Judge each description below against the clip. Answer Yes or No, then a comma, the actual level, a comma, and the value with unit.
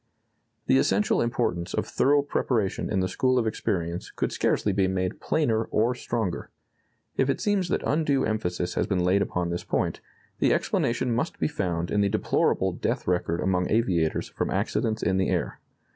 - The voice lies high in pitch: No, low, 100 Hz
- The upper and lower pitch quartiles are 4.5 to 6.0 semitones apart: Yes, average, 5.3 semitones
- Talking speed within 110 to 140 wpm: No, average, 175 wpm